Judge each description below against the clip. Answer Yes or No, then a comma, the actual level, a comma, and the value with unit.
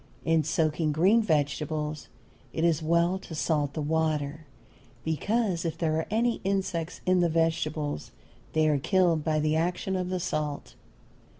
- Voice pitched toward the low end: No, medium, 160 Hz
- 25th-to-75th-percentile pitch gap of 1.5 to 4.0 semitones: Yes, narrow, 2.6 semitones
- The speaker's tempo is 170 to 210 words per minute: No, average, 155 wpm